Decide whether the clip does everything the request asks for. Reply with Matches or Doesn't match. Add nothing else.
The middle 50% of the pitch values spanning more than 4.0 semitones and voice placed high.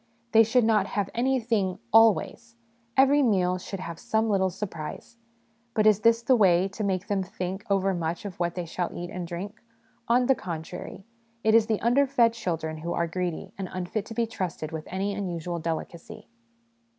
Matches